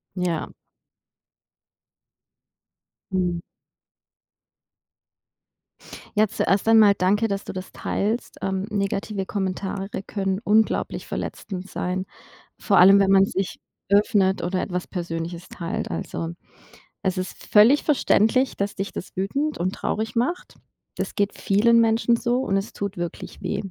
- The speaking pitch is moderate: No, high, 195 Hz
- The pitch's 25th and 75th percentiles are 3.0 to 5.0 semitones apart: No, narrow, 2.6 semitones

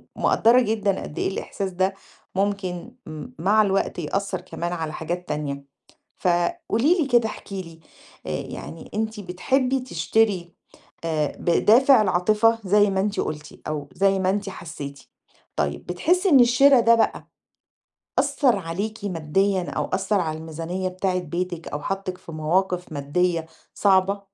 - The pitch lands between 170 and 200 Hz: Yes, high, 190 Hz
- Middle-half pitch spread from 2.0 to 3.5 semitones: No, average, 4.2 semitones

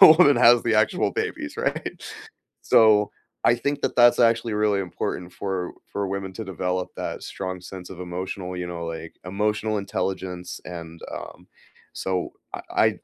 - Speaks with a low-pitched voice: Yes, very low, 95 Hz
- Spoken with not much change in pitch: No, average, 3.2 semitones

